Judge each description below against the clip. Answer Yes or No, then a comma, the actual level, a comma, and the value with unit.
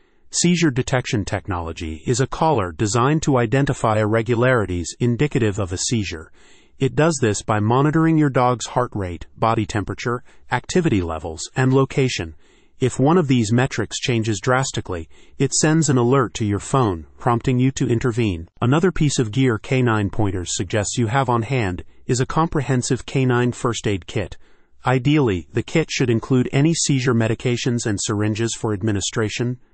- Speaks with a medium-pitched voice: No, low, 120 Hz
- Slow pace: No, average, 155 wpm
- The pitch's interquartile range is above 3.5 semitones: Yes, average, 4.2 semitones